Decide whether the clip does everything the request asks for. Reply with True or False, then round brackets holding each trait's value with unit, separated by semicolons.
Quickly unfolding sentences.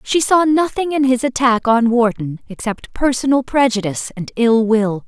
False (165 wpm)